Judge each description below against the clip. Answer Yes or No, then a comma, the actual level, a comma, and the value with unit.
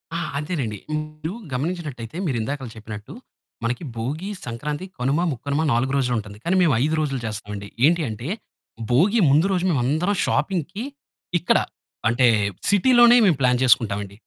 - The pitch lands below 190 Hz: Yes, medium, 140 Hz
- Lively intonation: Yes, wide, 6.2 semitones